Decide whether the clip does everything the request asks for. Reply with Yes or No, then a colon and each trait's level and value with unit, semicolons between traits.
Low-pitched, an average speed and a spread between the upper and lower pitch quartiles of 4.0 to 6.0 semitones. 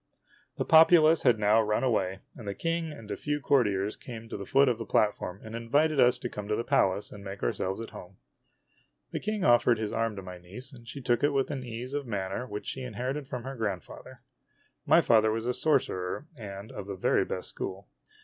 No: low, 115 Hz; fast, 225 wpm; average, 4.7 semitones